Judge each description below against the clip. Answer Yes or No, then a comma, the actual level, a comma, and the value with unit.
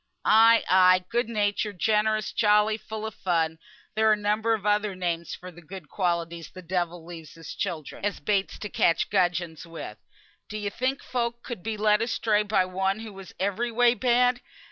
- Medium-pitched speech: No, high, 205 Hz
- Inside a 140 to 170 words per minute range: No, average, 185 wpm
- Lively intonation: No, average, 3.5 semitones